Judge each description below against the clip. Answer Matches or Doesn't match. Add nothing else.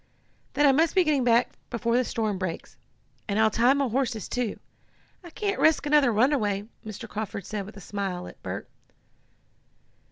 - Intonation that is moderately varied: Matches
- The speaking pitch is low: Doesn't match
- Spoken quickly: Doesn't match